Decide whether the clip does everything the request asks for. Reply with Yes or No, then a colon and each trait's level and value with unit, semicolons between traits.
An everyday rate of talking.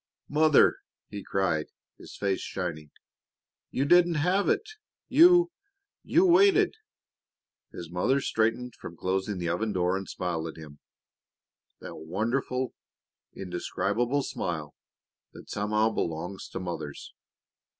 No: slow, 115 wpm